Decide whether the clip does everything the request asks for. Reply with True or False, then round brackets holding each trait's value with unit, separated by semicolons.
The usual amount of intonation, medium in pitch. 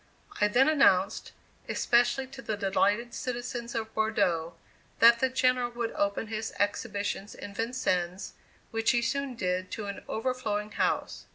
False (3.3 semitones; 225 Hz)